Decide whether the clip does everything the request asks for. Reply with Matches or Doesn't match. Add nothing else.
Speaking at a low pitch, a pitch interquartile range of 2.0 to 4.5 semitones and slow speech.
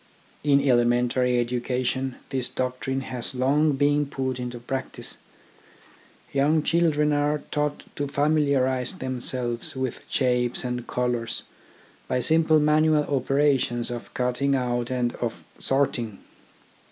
Matches